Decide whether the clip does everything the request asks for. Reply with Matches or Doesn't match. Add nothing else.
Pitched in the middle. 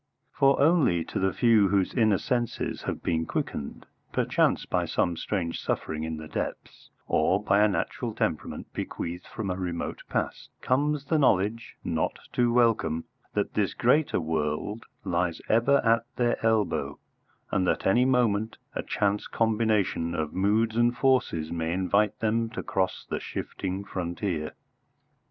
Doesn't match